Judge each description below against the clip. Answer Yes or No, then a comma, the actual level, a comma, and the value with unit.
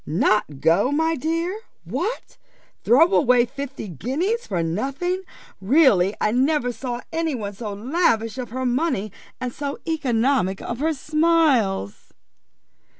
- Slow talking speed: Yes, slow, 130 wpm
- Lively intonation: Yes, wide, 6.9 semitones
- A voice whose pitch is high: Yes, very high, 255 Hz